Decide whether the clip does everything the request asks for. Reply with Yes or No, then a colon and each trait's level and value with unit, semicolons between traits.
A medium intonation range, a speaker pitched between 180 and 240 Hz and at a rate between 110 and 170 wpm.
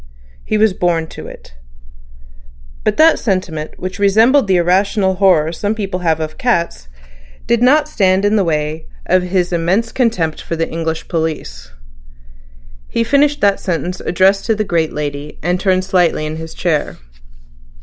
Yes: average, 4.2 semitones; medium, 185 Hz; average, 160 wpm